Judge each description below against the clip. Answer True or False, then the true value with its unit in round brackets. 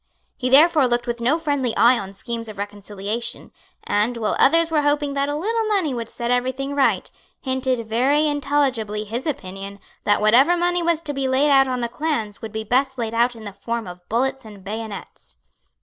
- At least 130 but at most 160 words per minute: False (195 wpm)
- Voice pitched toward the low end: False (250 Hz)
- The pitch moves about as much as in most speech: True (4.7 semitones)